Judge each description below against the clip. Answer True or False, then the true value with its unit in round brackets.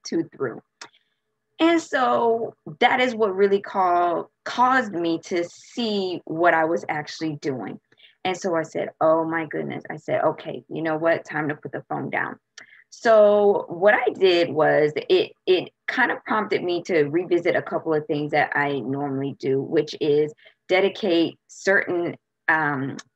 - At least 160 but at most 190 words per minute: True (165 wpm)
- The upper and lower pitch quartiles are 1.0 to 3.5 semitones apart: False (4.9 semitones)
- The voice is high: False (175 Hz)